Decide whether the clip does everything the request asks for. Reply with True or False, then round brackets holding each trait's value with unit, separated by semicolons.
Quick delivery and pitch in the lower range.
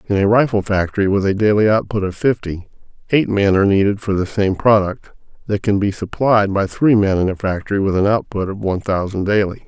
True (215 wpm; 100 Hz)